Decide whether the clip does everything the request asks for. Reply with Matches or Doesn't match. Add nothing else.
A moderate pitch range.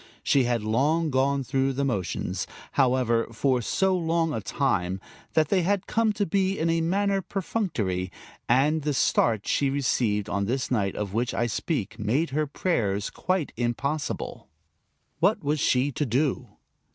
Doesn't match